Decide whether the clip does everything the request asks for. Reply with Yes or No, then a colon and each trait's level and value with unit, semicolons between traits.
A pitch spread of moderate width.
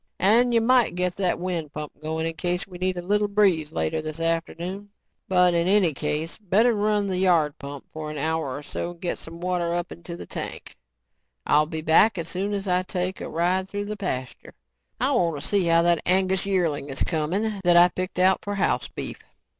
Yes: average, 3.1 semitones